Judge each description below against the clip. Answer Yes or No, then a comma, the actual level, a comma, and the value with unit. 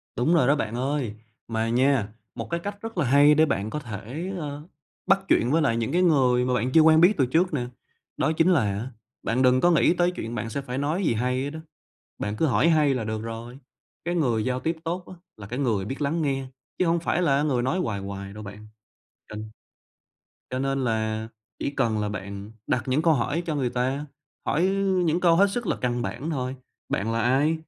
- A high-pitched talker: No, low, 130 Hz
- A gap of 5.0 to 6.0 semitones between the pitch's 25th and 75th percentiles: Yes, wide, 5.6 semitones